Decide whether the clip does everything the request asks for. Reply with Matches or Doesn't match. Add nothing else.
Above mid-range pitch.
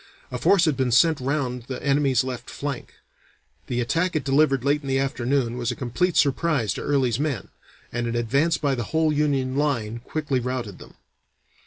Doesn't match